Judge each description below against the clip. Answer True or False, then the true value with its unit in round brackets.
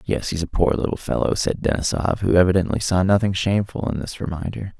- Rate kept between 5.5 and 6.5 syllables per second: True (6.0 syllables/s)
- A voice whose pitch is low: True (90 Hz)